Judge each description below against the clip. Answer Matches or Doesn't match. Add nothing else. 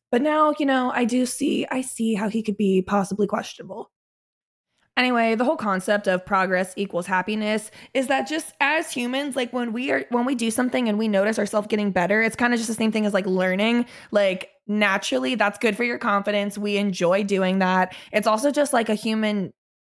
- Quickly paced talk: Matches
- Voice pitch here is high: Matches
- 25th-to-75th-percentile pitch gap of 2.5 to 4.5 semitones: Matches